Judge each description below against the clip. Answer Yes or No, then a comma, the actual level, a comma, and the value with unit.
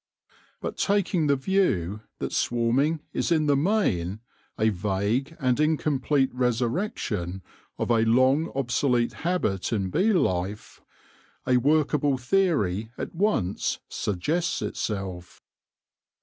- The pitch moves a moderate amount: No, wide, 7.0 semitones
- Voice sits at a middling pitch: No, low, 130 Hz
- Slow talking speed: Yes, slow, 110 wpm